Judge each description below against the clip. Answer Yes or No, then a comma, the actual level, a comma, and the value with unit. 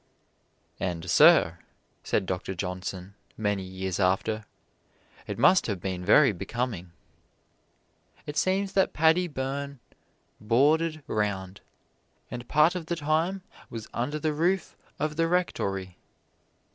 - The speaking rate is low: Yes, slow, 120 wpm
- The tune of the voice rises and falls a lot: Yes, wide, 8.7 semitones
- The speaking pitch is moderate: No, low, 120 Hz